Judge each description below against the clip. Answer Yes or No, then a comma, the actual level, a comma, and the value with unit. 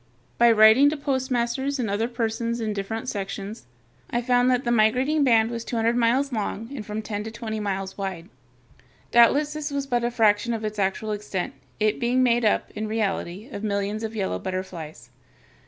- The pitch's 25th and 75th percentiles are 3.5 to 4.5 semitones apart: No, average, 2.7 semitones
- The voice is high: Yes, high, 225 Hz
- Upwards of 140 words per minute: Yes, average, 190 wpm